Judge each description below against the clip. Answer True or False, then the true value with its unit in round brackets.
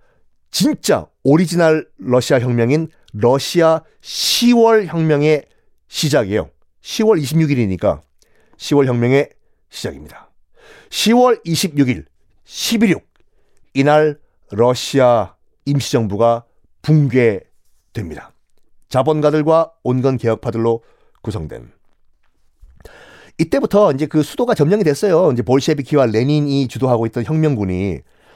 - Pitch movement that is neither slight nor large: True (4.7 semitones)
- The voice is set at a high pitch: False (140 Hz)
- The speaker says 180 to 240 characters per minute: True (225 characters per minute)